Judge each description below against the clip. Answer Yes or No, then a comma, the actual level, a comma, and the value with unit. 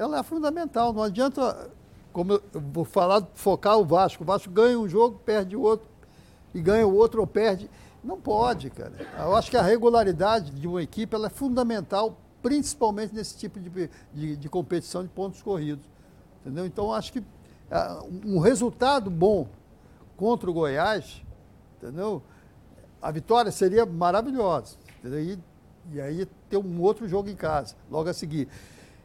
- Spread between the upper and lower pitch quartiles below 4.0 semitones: No, average, 4.7 semitones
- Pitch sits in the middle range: No, high, 195 Hz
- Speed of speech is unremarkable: Yes, average, 160 wpm